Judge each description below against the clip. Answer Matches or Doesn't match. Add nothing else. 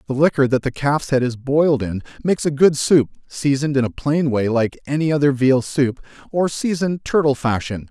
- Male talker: Matches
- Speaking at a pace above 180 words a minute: Matches